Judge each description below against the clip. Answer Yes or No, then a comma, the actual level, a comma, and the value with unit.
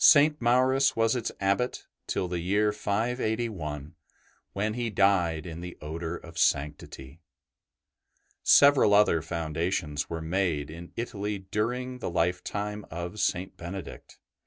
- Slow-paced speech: Yes, slow, 125 wpm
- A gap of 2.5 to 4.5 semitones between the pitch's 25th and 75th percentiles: No, average, 5.0 semitones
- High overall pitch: No, very low, 95 Hz